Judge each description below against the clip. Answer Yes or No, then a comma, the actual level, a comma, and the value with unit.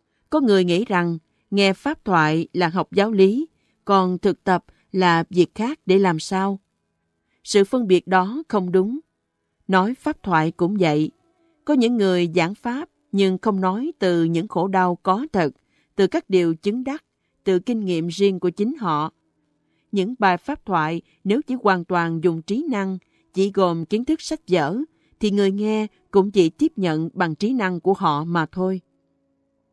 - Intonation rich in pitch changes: No, average, 3.7 semitones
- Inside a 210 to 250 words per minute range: No, average, 180 wpm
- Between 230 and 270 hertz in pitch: No, high, 190 Hz